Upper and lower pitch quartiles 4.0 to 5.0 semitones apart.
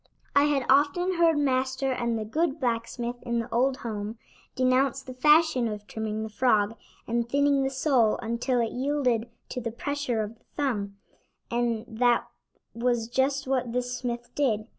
No: average, 3.0 semitones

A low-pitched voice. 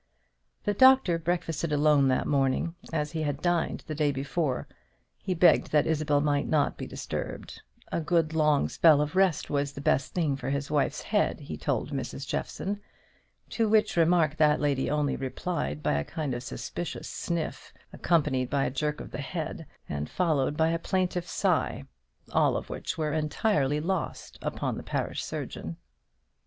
No: medium, 150 Hz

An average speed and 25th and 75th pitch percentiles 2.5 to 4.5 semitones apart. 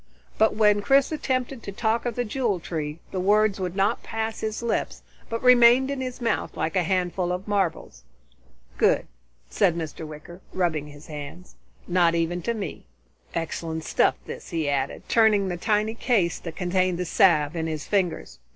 No: average, 175 wpm; average, 5.0 semitones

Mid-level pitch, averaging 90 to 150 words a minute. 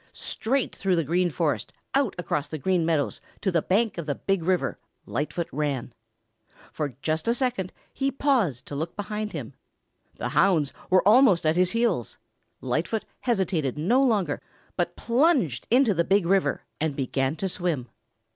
No: medium, 180 Hz; average, 160 wpm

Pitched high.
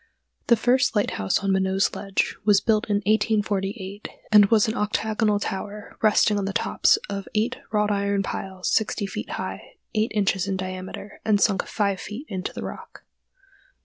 Yes: high, 205 Hz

